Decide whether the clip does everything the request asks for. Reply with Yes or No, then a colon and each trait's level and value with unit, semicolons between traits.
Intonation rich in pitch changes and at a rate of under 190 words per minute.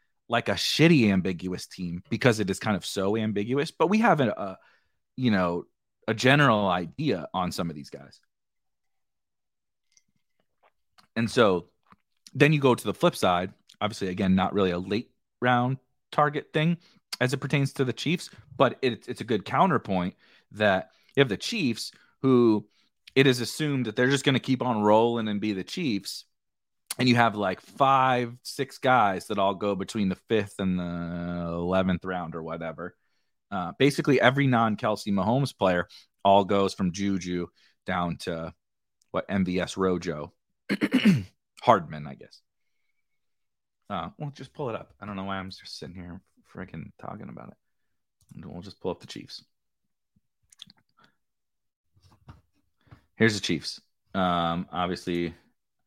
Yes: wide, 6.0 semitones; average, 155 wpm